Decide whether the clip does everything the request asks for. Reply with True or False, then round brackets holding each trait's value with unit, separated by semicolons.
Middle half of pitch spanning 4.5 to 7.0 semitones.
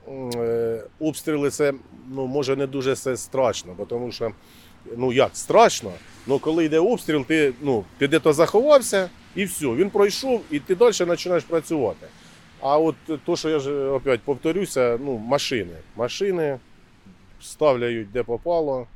True (5.2 semitones)